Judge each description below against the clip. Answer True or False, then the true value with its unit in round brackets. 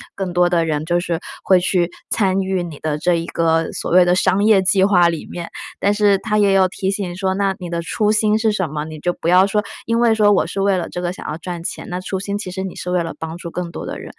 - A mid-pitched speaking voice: True (180 Hz)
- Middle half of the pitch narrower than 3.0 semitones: True (2.6 semitones)